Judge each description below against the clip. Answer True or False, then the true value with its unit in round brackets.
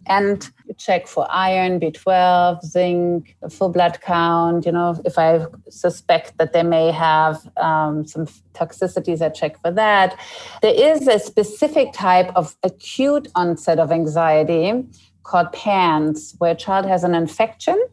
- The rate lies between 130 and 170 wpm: True (145 wpm)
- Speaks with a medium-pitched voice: True (175 Hz)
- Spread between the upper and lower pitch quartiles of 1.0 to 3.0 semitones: True (2.5 semitones)